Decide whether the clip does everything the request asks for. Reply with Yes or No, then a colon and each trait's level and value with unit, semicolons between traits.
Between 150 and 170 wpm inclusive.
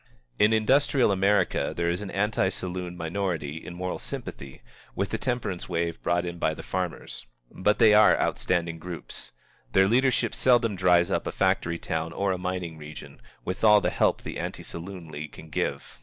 No: average, 180 wpm